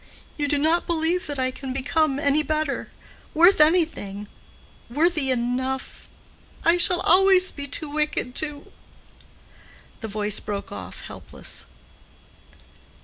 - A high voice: Yes, very high, 290 Hz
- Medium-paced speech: No, slow, 105 wpm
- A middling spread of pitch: Yes, average, 4.0 semitones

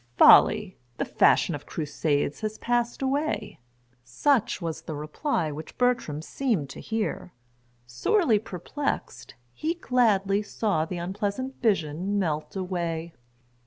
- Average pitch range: No, wide, 7.0 semitones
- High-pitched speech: Yes, high, 200 Hz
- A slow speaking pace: Yes, slow, 120 wpm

